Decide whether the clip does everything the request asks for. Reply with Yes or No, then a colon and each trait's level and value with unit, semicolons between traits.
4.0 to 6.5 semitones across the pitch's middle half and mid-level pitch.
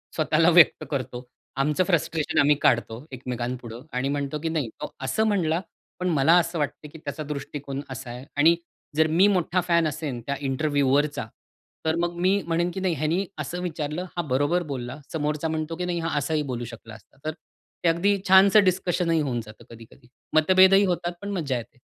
Yes: average, 4.3 semitones; medium, 155 Hz